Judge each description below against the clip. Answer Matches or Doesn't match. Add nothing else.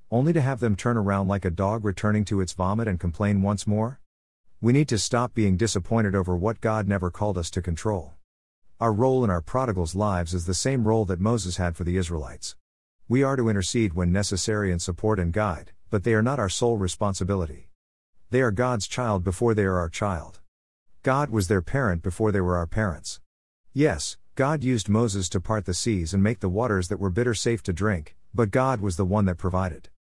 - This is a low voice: Matches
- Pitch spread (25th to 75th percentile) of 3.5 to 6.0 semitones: Matches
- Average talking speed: Doesn't match